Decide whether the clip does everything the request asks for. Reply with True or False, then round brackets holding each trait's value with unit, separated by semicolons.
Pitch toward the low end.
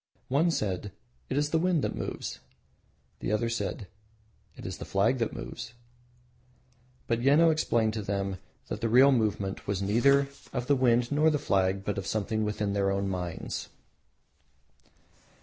True (110 Hz)